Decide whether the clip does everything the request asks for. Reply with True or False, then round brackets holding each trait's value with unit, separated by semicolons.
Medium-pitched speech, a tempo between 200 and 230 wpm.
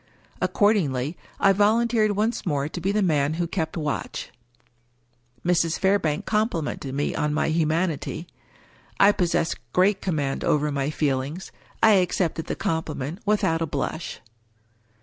False (165 Hz; 135 wpm)